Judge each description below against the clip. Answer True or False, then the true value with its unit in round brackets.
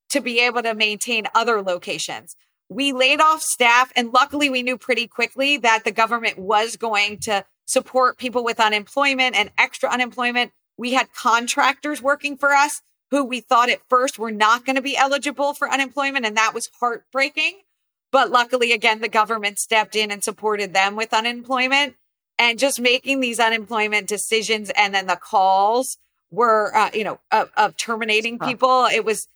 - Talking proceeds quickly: False (175 wpm)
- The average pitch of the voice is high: True (240 Hz)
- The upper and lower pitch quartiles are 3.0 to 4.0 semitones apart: True (3.3 semitones)